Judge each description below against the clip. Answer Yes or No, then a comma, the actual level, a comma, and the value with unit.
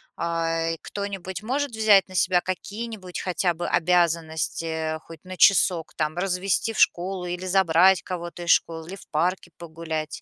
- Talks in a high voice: No, medium, 180 Hz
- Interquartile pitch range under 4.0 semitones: Yes, narrow, 2.6 semitones